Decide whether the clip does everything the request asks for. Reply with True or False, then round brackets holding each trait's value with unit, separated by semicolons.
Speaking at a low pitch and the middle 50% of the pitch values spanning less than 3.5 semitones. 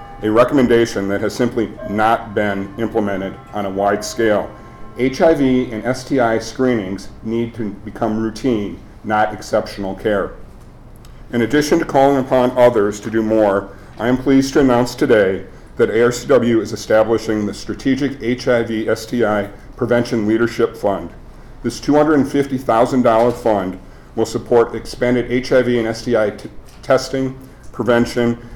True (115 Hz; 2.9 semitones)